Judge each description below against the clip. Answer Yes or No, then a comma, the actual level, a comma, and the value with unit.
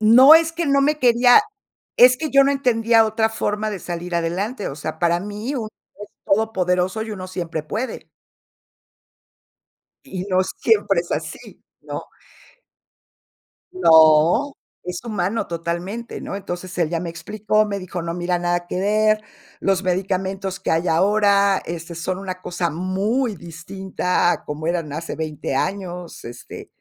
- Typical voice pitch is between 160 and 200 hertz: Yes, high, 190 Hz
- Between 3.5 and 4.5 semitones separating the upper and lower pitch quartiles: Yes, average, 4.0 semitones